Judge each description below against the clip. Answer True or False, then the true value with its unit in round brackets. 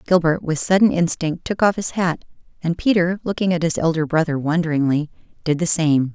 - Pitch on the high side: False (165 Hz)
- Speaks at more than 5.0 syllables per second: True (5.5 syllables/s)